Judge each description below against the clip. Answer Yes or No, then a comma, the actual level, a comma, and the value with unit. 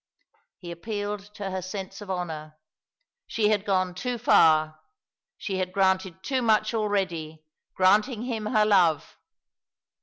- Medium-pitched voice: No, high, 195 Hz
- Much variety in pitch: No, average, 3.0 semitones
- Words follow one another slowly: Yes, slow, 130 wpm